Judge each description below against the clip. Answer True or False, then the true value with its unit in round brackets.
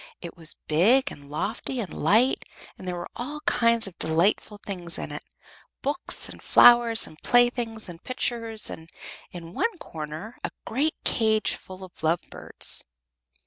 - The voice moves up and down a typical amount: False (6.1 semitones)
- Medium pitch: False (210 Hz)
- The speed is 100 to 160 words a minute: True (150 wpm)